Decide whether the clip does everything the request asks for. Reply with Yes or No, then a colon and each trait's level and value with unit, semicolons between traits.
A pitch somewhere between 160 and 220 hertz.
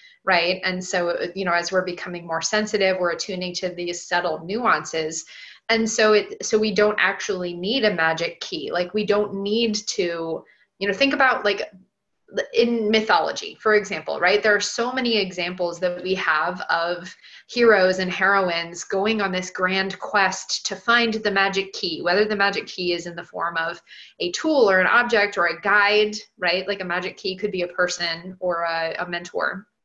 Yes: high, 190 Hz